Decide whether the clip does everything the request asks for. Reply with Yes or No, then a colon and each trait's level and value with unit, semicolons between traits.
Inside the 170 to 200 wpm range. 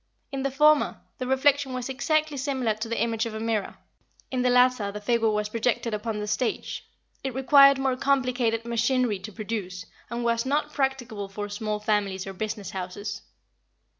Yes: average, 175 wpm